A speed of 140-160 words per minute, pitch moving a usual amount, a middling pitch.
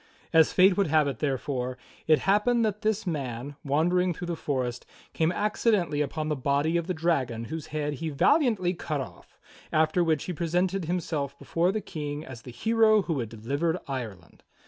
No: average, 185 wpm; average, 4.4 semitones; medium, 160 Hz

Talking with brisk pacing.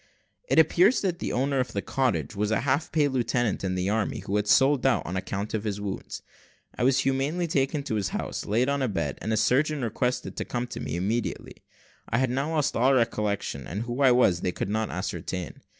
Yes: fast, 225 wpm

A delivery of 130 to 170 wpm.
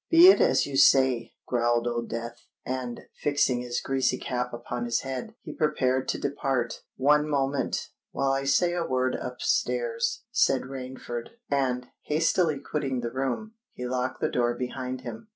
Yes: average, 160 wpm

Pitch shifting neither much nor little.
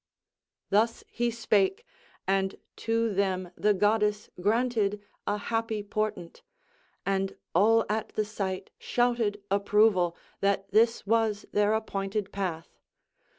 No: narrow, 2.3 semitones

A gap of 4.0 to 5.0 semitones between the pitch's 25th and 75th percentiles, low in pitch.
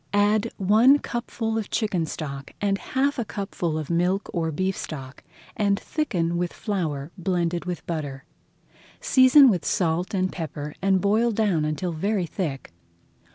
No: average, 4.6 semitones; medium, 185 Hz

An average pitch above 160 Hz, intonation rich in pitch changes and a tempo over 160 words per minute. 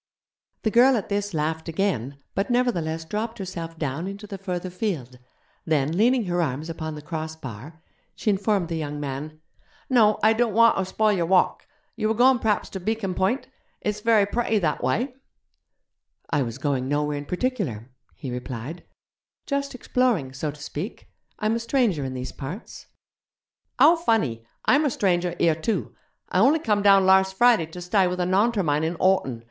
Yes: medium, 185 Hz; wide, 6.1 semitones; average, 175 wpm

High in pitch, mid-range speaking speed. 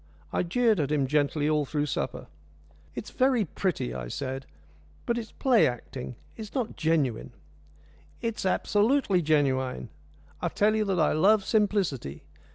No: medium, 165 Hz; average, 155 wpm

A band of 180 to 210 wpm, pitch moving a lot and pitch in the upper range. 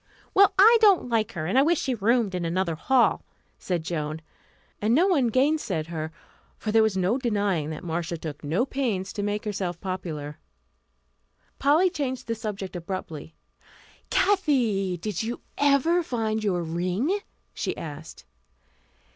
No: average, 150 wpm; wide, 7.2 semitones; high, 205 Hz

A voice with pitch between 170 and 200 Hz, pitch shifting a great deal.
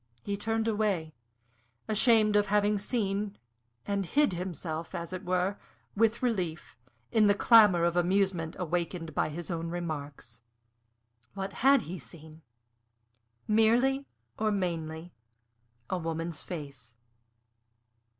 No: medium, 185 Hz; average, 4.2 semitones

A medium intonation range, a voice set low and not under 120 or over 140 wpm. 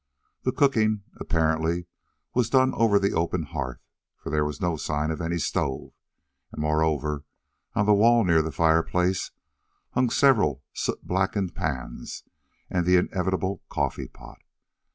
Yes: average, 4.7 semitones; very low, 85 Hz; slow, 135 wpm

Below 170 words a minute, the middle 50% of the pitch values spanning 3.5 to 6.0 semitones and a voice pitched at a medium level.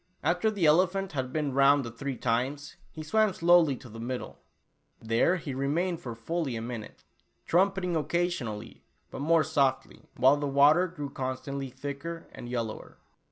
Yes: average, 160 wpm; average, 4.7 semitones; medium, 145 Hz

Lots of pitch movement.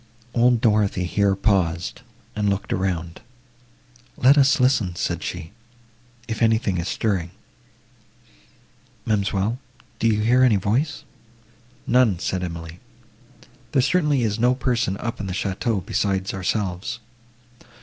No: average, 4.4 semitones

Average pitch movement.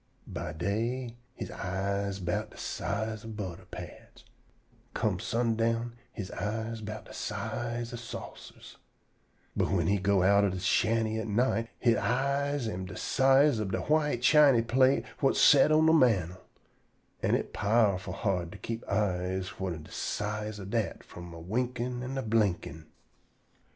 Yes: average, 3.8 semitones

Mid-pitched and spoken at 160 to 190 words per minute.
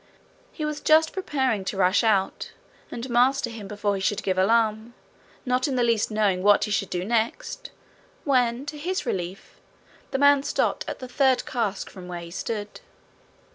No: high, 230 Hz; average, 175 wpm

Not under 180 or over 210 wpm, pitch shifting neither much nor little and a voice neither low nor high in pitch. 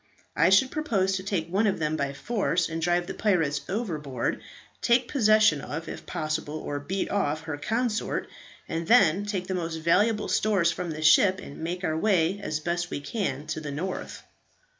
Yes: average, 185 wpm; average, 4.5 semitones; medium, 175 Hz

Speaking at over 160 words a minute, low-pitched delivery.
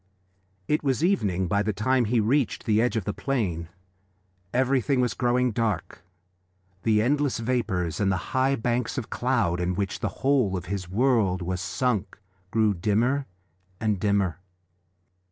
No: average, 155 wpm; low, 110 Hz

